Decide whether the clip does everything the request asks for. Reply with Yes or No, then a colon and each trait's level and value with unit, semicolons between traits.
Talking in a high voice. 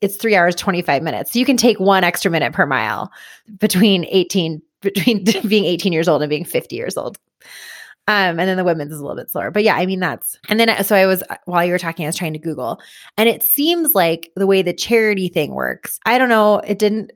Yes: high, 195 Hz